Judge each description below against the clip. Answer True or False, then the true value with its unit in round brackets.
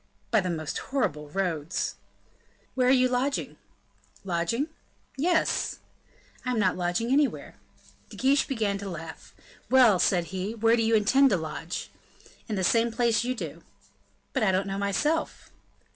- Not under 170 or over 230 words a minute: False (155 wpm)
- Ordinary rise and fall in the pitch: False (5.7 semitones)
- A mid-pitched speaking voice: False (215 Hz)